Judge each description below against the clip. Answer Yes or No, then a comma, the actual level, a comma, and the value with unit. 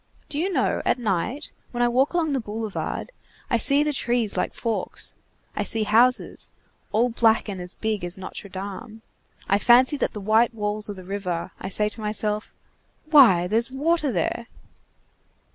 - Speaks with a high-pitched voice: Yes, high, 220 Hz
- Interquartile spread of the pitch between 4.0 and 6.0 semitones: No, average, 3.5 semitones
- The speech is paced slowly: No, average, 175 wpm